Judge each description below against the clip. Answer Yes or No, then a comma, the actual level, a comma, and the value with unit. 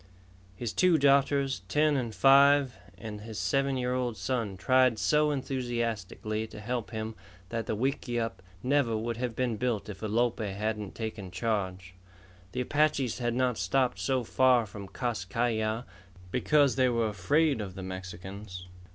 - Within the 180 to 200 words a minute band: No, average, 155 wpm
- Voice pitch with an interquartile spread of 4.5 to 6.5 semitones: No, average, 3.5 semitones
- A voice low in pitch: Yes, low, 120 Hz